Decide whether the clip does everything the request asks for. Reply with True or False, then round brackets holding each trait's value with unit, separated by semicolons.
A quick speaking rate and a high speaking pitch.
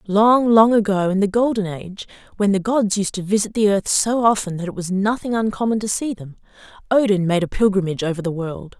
True (220 wpm; 200 Hz)